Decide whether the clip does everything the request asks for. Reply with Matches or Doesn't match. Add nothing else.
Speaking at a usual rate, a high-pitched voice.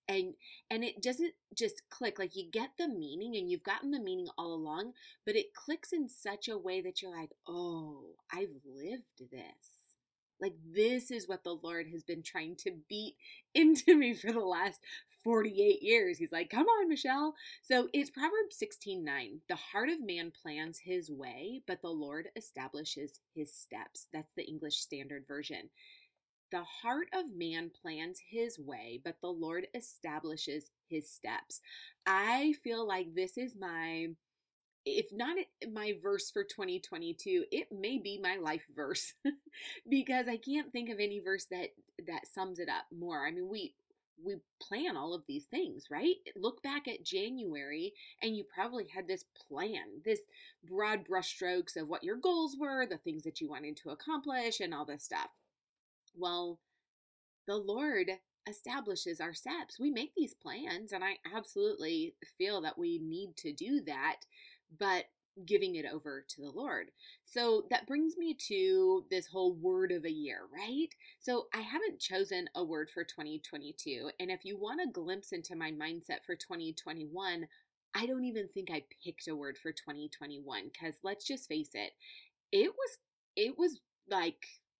Matches